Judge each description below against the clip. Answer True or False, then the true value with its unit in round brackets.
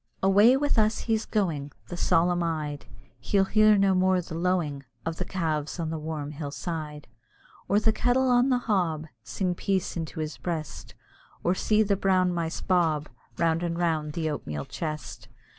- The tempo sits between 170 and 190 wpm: True (175 wpm)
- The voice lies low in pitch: False (175 Hz)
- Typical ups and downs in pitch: True (4.0 semitones)